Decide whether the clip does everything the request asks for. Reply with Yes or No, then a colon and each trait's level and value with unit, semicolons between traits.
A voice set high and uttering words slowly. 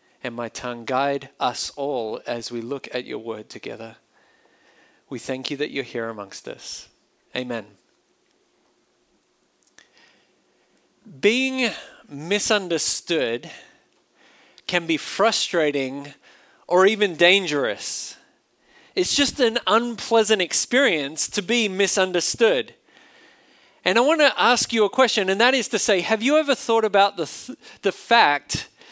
Yes: high, 195 Hz; slow, 125 wpm